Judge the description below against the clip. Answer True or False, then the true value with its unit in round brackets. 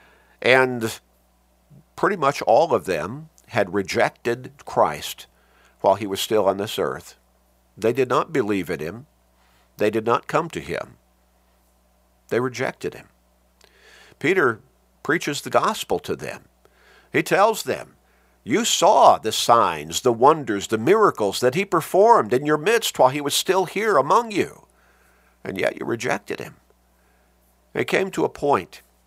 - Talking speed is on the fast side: False (145 wpm)